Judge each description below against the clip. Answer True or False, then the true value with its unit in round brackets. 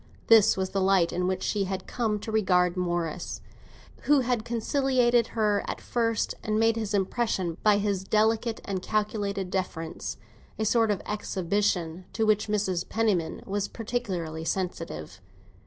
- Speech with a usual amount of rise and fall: True (3.3 semitones)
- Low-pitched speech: False (205 Hz)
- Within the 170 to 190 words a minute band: False (145 wpm)